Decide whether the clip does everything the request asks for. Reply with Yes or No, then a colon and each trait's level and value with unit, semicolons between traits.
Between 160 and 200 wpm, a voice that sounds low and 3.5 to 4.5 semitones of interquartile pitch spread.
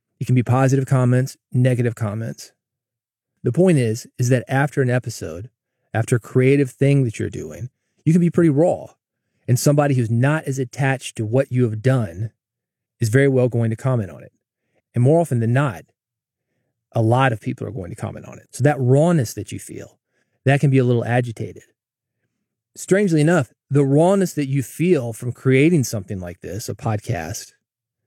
No: average, 185 wpm; low, 125 Hz; average, 3.0 semitones